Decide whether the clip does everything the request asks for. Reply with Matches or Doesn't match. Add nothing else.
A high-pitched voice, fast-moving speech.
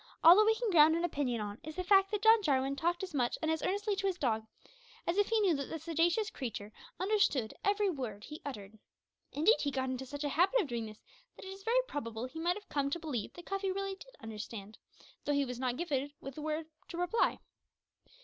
Matches